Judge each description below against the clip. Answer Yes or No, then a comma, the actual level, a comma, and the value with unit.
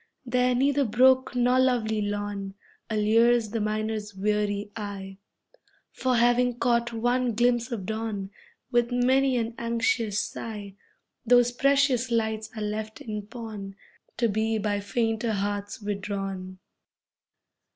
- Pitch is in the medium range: No, high, 225 Hz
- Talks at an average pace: No, slow, 120 wpm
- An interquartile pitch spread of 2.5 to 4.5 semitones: Yes, average, 2.8 semitones